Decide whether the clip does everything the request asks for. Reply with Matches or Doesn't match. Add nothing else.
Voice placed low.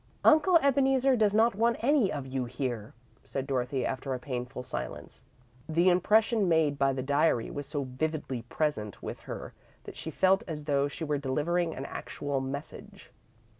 Doesn't match